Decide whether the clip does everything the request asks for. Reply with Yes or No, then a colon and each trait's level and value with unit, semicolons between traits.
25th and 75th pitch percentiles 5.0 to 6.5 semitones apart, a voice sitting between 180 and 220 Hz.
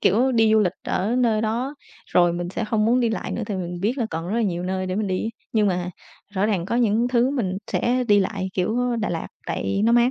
No: average, 4.1 semitones; high, 215 Hz